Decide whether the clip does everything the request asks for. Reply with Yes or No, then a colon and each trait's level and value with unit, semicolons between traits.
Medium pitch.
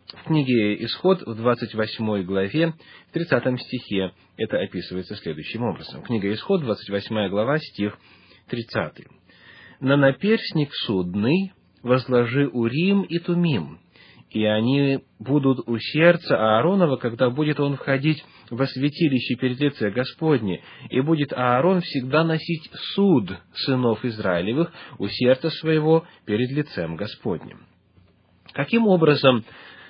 No: low, 130 Hz